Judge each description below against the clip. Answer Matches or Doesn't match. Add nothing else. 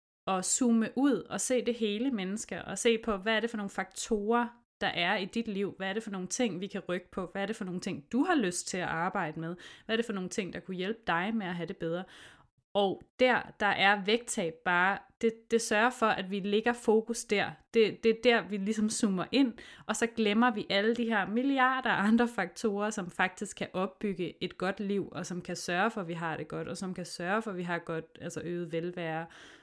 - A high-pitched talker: Matches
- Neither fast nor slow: Doesn't match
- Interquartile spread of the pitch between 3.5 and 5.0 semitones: Matches